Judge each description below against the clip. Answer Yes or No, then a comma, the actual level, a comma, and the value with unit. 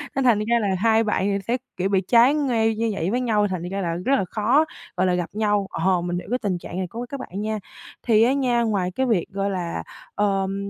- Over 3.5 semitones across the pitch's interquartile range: Yes, average, 4.0 semitones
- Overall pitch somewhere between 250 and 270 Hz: No, high, 210 Hz